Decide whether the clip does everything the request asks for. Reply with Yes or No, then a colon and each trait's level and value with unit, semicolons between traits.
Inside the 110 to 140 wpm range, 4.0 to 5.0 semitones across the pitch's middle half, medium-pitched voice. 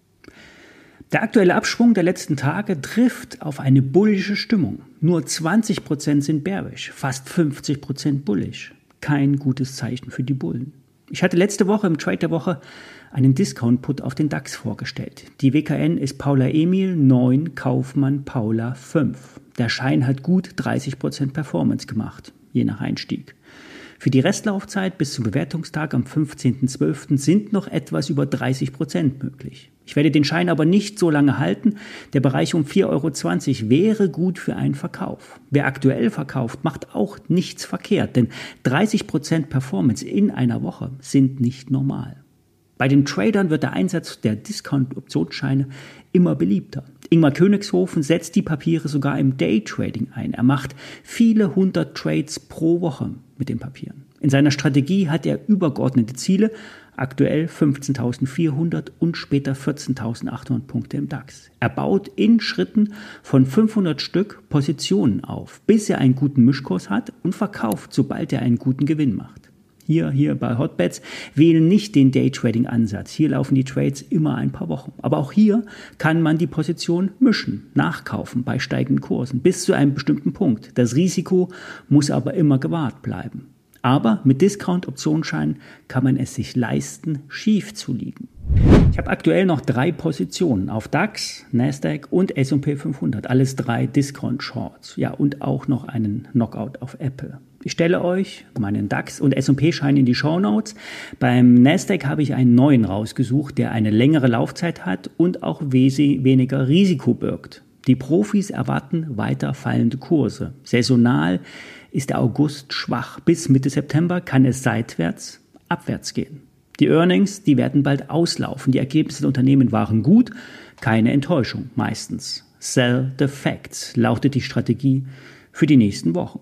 No: average, 150 wpm; average, 4.6 semitones; medium, 145 Hz